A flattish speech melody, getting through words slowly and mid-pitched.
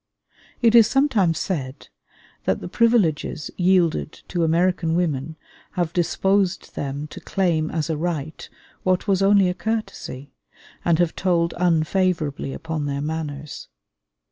No: average, 3.3 semitones; slow, 130 wpm; medium, 170 Hz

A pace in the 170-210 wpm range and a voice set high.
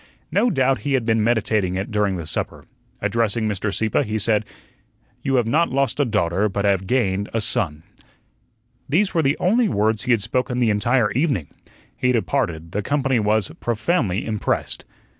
No: average, 175 wpm; low, 110 Hz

